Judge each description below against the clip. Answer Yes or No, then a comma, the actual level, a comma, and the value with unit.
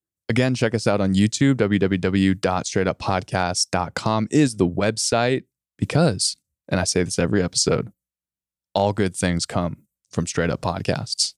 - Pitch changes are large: No, average, 3.4 semitones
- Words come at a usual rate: No, slow, 130 wpm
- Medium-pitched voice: No, very low, 95 Hz